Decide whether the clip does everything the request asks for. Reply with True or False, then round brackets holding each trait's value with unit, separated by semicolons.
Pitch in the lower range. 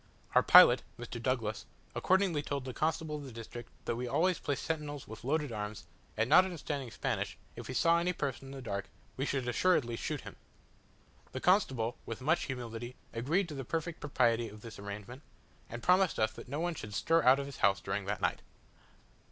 True (130 Hz)